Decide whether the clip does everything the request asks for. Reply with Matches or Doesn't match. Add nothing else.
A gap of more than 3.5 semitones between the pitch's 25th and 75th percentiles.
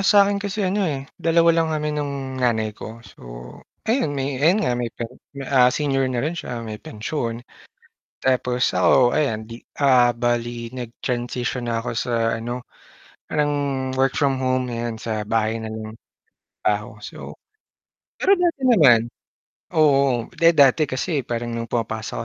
Matches